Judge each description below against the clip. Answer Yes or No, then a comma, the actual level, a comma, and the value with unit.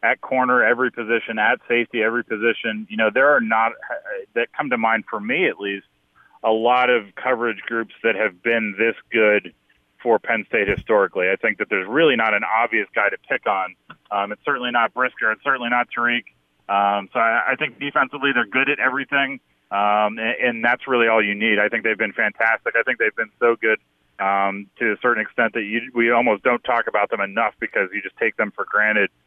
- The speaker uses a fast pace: Yes, fast, 215 wpm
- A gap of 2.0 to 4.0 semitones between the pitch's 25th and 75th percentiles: Yes, average, 2.8 semitones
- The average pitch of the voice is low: Yes, low, 115 Hz